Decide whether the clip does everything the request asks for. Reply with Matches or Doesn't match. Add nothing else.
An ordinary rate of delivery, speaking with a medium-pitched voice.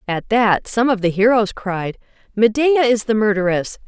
Doesn't match